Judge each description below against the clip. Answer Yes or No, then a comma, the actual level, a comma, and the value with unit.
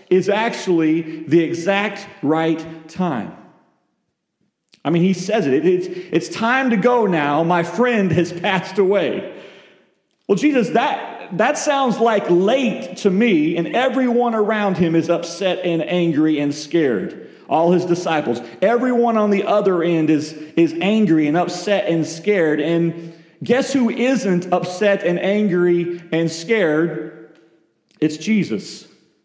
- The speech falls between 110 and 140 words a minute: Yes, slow, 135 wpm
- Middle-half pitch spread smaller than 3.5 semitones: No, average, 4.5 semitones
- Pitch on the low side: No, medium, 175 Hz